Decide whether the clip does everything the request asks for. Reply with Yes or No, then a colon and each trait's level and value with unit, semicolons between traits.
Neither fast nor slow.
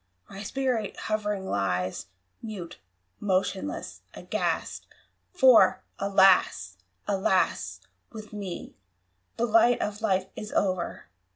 No: slow, 95 wpm